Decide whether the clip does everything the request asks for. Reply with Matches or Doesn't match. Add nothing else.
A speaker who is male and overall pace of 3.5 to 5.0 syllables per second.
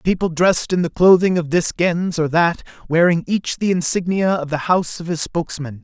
Doesn't match